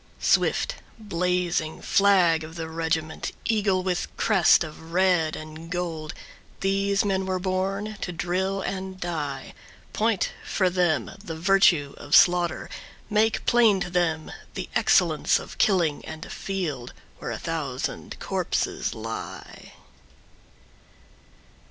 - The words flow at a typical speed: No, slow, 120 wpm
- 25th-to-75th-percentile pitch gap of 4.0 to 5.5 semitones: No, average, 3.3 semitones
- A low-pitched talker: No, medium, 180 Hz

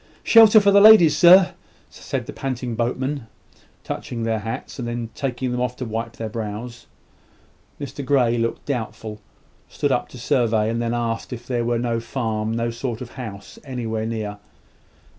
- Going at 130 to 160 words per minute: No, average, 170 wpm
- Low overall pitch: Yes, low, 120 Hz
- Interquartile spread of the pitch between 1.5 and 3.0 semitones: Yes, narrow, 2.5 semitones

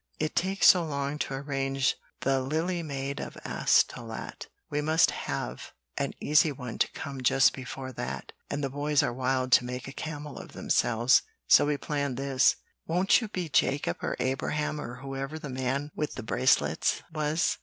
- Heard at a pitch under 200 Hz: Yes, medium, 140 Hz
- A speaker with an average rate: Yes, average, 175 wpm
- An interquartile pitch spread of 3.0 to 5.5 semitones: No, narrow, 2.6 semitones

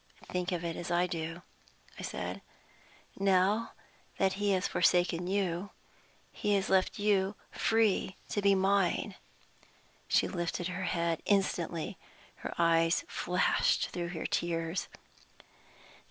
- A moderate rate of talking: No, slow, 125 wpm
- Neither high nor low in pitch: Yes, medium, 180 Hz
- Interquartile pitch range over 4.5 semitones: No, narrow, 2.4 semitones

